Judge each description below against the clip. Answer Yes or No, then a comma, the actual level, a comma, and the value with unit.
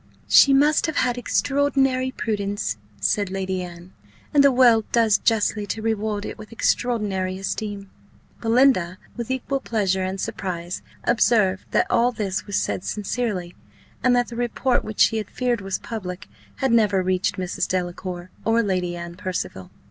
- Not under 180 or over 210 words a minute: No, average, 155 wpm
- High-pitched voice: Yes, high, 210 Hz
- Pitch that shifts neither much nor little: Yes, average, 4.5 semitones